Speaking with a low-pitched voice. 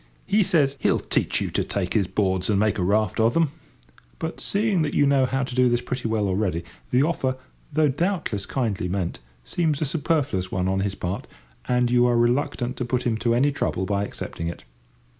Yes: low, 120 Hz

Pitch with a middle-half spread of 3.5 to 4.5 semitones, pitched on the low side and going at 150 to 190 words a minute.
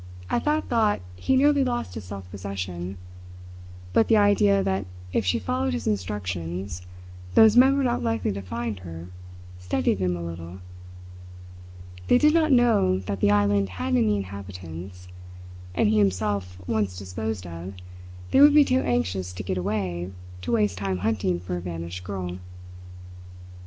Yes: average, 4.1 semitones; very low, 95 Hz; average, 155 wpm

